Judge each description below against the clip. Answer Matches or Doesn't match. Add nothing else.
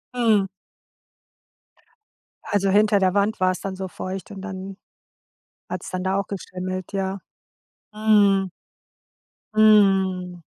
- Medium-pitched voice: Doesn't match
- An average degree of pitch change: Doesn't match